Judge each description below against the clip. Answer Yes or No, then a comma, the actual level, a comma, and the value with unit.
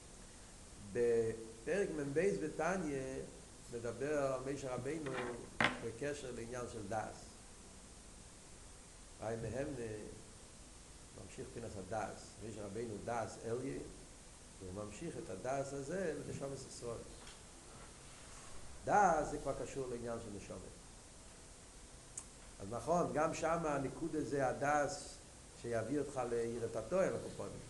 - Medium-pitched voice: No, low, 115 Hz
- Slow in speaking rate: Yes, slow, 95 wpm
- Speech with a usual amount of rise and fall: Yes, average, 4.8 semitones